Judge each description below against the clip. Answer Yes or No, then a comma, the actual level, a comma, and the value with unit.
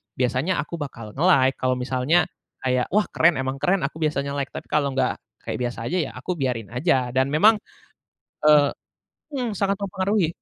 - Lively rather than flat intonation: Yes, wide, 5.7 semitones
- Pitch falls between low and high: Yes, medium, 145 Hz